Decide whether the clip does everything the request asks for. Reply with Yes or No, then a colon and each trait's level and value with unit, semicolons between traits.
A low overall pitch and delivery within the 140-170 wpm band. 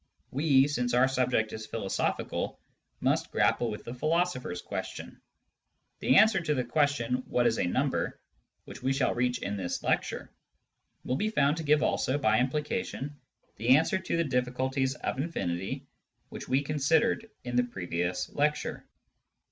Yes: low, 130 Hz; average, 160 wpm